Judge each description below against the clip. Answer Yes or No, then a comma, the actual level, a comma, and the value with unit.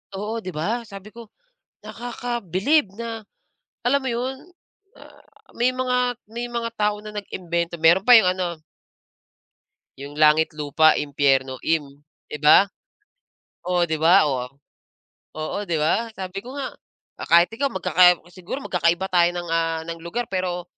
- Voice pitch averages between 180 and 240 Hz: Yes, medium, 185 Hz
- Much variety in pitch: Yes, wide, 5.9 semitones